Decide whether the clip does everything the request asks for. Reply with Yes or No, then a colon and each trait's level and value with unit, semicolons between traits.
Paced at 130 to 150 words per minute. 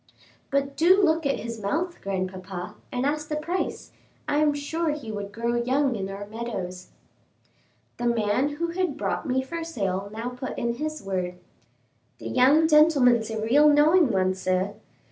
No: average, 165 wpm